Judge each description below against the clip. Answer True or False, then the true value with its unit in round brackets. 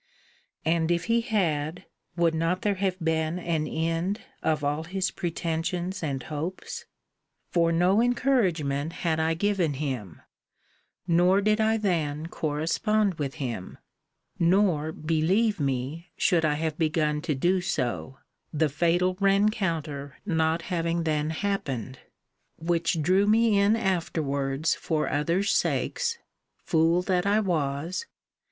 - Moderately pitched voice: True (165 Hz)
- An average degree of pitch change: True (3.7 semitones)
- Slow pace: True (125 wpm)